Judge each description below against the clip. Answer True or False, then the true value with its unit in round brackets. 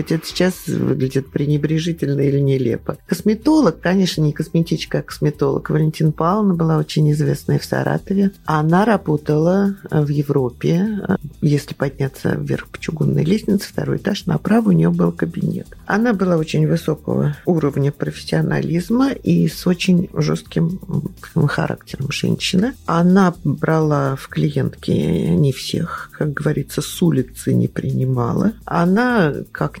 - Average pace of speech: True (125 wpm)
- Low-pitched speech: False (160 Hz)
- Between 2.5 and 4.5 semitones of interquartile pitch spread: True (3.9 semitones)